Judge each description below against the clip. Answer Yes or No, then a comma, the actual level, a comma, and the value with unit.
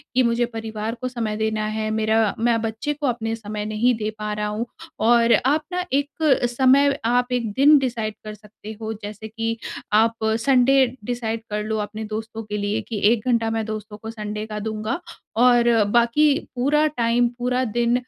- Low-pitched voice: No, high, 225 Hz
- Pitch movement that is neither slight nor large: No, narrow, 2.2 semitones